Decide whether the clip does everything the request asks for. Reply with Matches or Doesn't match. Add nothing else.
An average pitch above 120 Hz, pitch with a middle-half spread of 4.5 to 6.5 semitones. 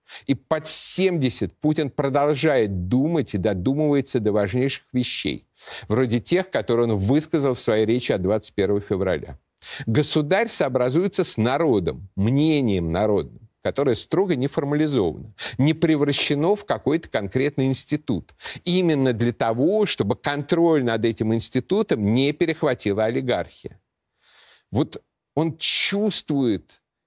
Matches